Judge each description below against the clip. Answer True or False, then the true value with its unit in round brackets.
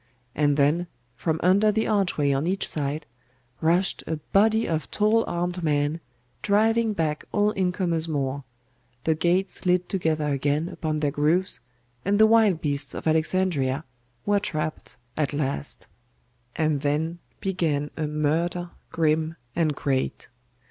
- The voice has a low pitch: False (160 Hz)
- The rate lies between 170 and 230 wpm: False (135 wpm)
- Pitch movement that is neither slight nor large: True (3.9 semitones)